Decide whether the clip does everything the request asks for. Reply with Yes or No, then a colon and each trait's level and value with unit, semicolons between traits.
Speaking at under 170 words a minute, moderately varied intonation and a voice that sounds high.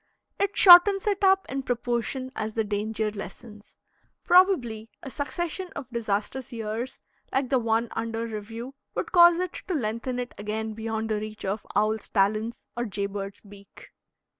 Yes: average, 160 wpm; average, 3.8 semitones; high, 225 Hz